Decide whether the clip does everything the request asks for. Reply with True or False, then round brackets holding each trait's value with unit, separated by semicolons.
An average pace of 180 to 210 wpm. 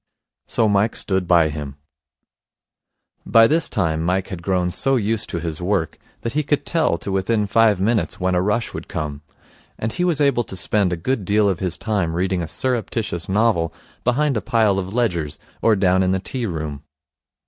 True (190 wpm)